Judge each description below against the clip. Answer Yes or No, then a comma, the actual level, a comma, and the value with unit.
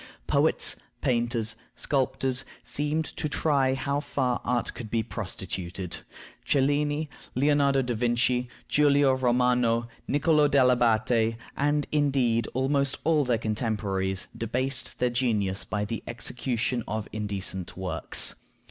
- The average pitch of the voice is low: Yes, low, 125 Hz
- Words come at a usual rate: No, slow, 115 wpm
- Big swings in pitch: No, average, 3.8 semitones